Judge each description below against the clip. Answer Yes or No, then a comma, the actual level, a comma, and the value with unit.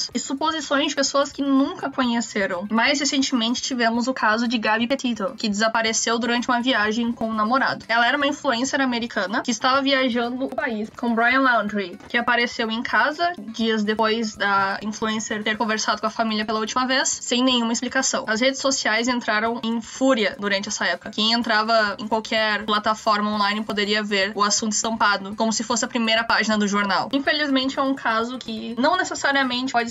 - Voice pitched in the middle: No, high, 235 Hz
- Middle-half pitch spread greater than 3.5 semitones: No, average, 3.2 semitones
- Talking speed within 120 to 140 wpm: No, fast, 185 wpm